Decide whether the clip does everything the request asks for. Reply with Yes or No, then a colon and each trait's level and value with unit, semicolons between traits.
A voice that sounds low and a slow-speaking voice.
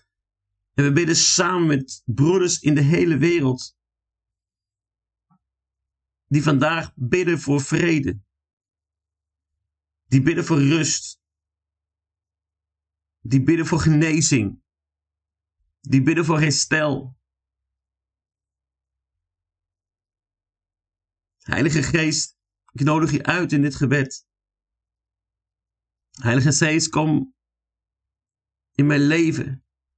Yes: low, 105 Hz; slow, 85 wpm